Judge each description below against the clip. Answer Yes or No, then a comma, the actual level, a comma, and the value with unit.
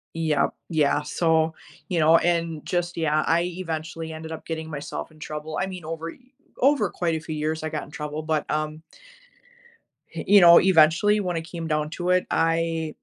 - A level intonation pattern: Yes, narrow, 1.6 semitones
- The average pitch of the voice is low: No, medium, 160 Hz